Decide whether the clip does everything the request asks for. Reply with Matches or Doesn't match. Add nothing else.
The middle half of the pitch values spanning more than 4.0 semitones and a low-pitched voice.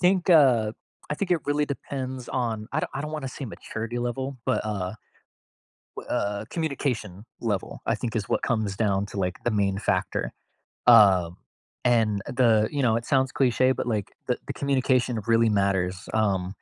Matches